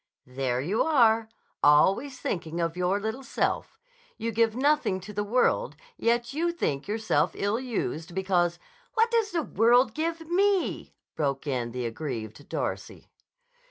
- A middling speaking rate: Yes, average, 145 wpm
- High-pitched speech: Yes, high, 215 Hz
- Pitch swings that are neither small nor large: No, wide, 8.8 semitones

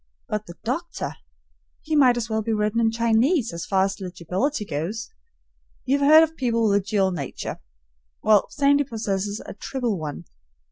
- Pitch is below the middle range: No, high, 220 Hz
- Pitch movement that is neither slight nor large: Yes, average, 5.0 semitones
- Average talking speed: Yes, average, 175 wpm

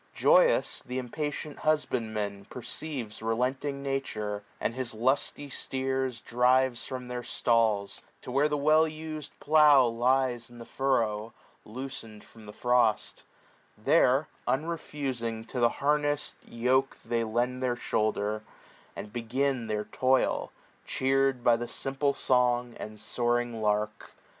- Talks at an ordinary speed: No, slow, 130 wpm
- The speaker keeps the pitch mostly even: No, average, 3.0 semitones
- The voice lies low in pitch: Yes, low, 125 Hz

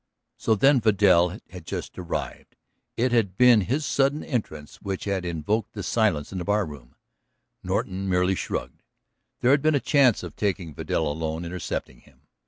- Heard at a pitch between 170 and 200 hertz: No, low, 100 Hz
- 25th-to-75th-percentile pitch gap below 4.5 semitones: No, average, 5.3 semitones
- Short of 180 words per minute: Yes, average, 165 wpm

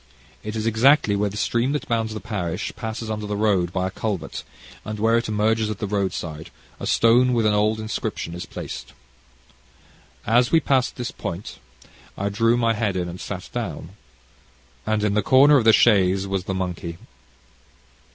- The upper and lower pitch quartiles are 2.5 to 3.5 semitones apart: Yes, average, 2.8 semitones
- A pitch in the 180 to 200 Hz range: No, low, 105 Hz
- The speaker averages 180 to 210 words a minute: Yes, average, 190 wpm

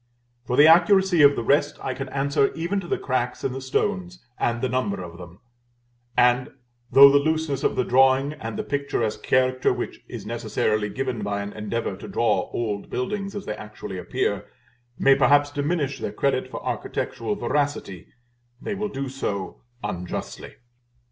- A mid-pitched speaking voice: No, low, 130 Hz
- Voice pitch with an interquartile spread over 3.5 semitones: Yes, average, 4.2 semitones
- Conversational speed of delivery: Yes, average, 170 wpm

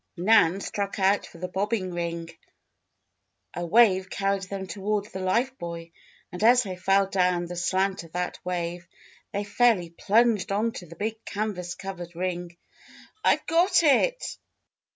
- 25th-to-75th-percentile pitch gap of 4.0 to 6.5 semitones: No, average, 3.0 semitones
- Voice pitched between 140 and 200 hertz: Yes, high, 190 Hz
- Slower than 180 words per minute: Yes, average, 150 wpm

